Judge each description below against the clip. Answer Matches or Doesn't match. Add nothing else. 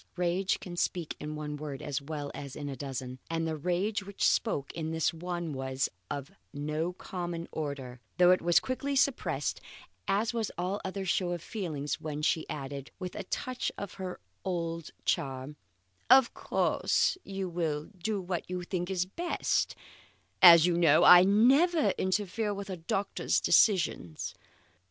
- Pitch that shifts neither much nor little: Matches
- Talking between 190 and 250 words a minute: Doesn't match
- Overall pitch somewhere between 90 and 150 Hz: Doesn't match